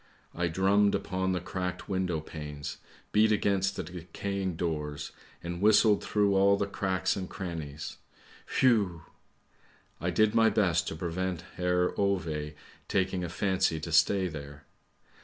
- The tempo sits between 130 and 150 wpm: Yes, average, 140 wpm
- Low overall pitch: Yes, very low, 90 Hz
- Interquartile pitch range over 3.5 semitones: No, average, 3.1 semitones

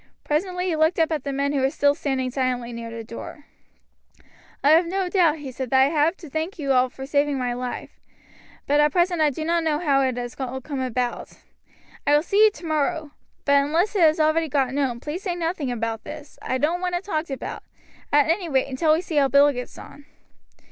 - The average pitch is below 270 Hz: No, very high, 290 Hz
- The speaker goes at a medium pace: No, fast, 225 wpm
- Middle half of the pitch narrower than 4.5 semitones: Yes, average, 3.8 semitones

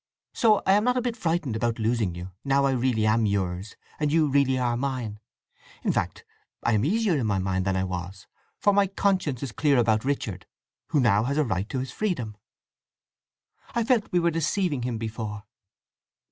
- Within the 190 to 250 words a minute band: Yes, average, 195 wpm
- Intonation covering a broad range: Yes, wide, 7.2 semitones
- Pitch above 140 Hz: No, low, 125 Hz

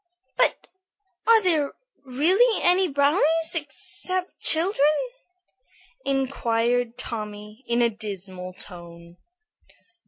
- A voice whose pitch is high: Yes, very high, 265 Hz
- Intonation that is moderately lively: No, wide, 7.6 semitones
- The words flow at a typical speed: No, slow, 85 wpm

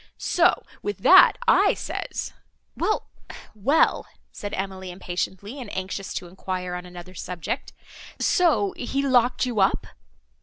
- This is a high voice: Yes, high, 195 Hz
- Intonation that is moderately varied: No, wide, 5.7 semitones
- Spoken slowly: Yes, slow, 120 wpm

